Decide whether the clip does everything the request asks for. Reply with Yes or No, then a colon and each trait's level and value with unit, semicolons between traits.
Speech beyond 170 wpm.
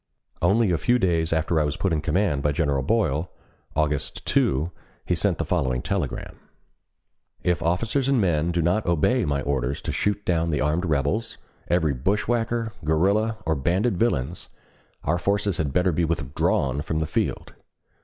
No: average, 165 wpm